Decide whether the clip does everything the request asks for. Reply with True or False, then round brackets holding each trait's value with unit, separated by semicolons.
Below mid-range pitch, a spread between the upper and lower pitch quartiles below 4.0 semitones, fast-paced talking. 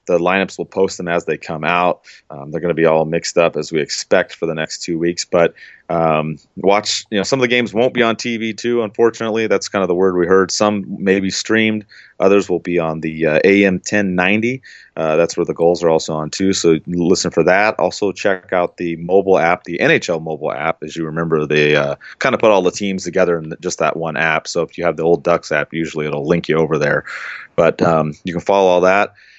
True (90 Hz; 3.5 semitones; 245 wpm)